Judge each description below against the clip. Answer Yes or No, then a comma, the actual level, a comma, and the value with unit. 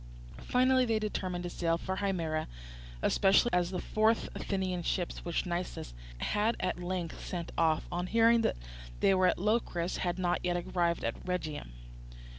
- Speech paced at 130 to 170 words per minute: Yes, average, 160 wpm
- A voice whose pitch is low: No, medium, 180 Hz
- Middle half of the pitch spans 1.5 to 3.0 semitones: Yes, average, 2.7 semitones